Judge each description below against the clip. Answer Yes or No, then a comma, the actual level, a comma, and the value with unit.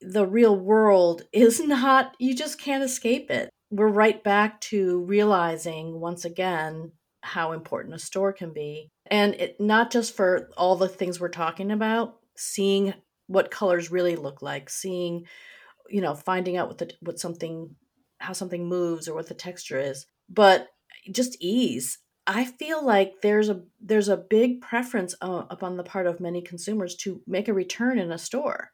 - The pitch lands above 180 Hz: Yes, high, 190 Hz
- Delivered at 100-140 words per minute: No, average, 170 wpm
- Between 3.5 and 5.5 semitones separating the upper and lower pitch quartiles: Yes, average, 3.8 semitones